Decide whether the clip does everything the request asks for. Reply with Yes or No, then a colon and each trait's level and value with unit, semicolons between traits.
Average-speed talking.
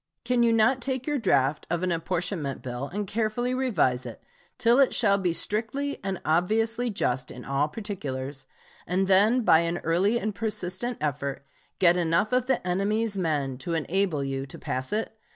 Yes: average, 175 wpm